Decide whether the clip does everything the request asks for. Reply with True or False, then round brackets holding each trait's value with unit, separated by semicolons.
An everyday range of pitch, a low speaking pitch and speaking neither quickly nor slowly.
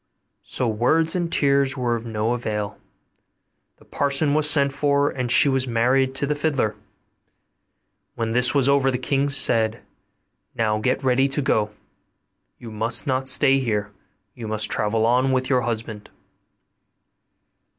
True (3.6 semitones; 130 Hz; 150 wpm)